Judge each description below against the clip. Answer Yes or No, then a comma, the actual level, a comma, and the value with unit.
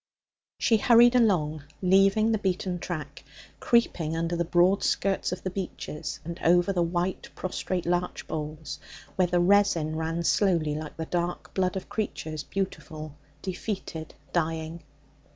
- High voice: No, medium, 175 Hz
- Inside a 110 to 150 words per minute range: Yes, average, 140 wpm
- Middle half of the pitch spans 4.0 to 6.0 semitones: No, average, 3.1 semitones